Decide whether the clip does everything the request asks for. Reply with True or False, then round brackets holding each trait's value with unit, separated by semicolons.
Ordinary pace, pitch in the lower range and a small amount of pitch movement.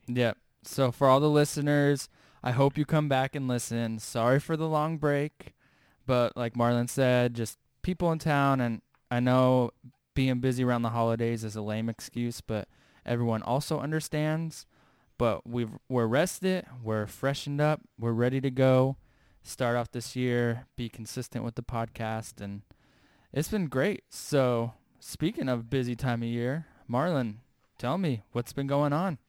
False (165 wpm; 125 Hz; 3.2 semitones)